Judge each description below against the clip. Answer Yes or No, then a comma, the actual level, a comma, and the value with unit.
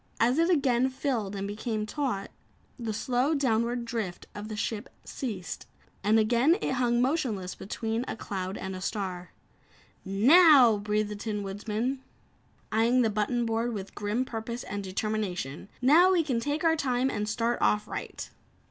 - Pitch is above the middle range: Yes, high, 225 Hz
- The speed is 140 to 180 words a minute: Yes, average, 160 wpm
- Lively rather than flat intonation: No, average, 3.7 semitones